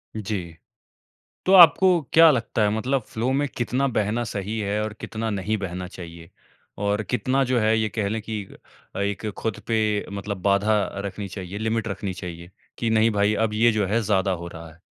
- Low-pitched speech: Yes, low, 105 Hz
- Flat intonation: Yes, narrow, 2.2 semitones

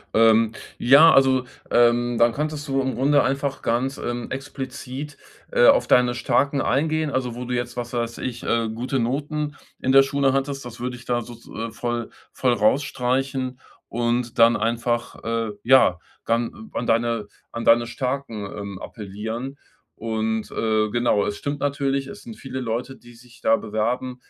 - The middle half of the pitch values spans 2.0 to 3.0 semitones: Yes, average, 2.7 semitones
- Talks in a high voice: No, low, 125 Hz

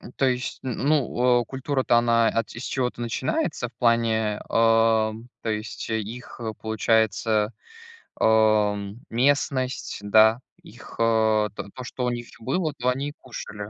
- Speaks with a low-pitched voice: Yes, low, 115 Hz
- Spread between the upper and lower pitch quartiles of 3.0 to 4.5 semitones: No, narrow, 2.4 semitones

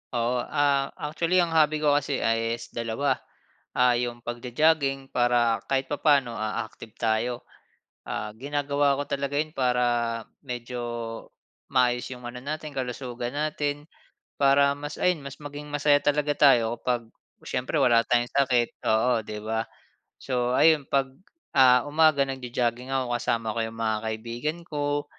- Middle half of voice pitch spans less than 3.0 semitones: No, average, 3.3 semitones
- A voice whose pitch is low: Yes, low, 130 Hz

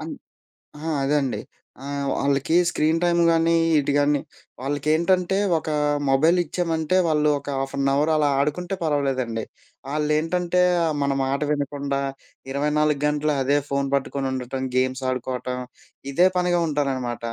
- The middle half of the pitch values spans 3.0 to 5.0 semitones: No, narrow, 2.6 semitones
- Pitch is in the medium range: Yes, medium, 145 Hz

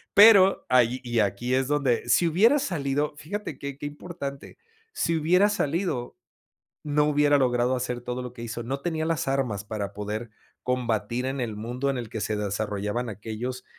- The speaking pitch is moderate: No, low, 125 Hz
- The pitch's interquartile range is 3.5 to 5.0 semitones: Yes, average, 4.2 semitones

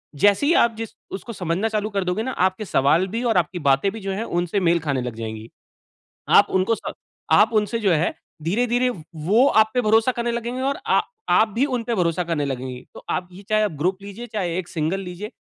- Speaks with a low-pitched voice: No, high, 195 Hz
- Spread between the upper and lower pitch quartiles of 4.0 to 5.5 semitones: Yes, average, 4.9 semitones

